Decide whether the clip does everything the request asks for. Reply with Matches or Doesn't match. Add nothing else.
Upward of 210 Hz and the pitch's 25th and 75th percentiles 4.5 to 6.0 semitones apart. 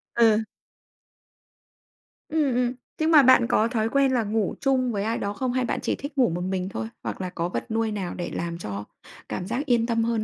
Matches